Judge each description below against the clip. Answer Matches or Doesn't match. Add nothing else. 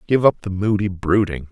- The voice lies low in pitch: Matches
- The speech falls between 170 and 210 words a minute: Matches